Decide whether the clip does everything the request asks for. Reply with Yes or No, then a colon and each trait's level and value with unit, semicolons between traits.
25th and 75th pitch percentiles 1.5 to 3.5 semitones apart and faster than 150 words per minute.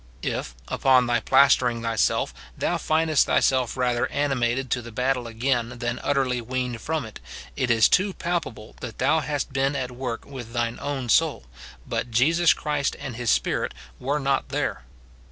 Yes: average, 2.7 semitones; average, 170 wpm